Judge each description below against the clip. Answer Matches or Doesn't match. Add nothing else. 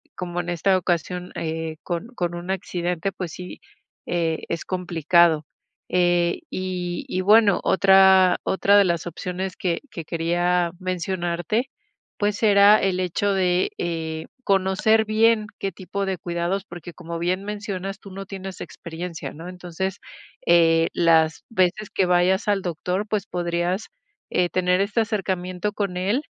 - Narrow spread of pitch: Matches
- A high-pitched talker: Doesn't match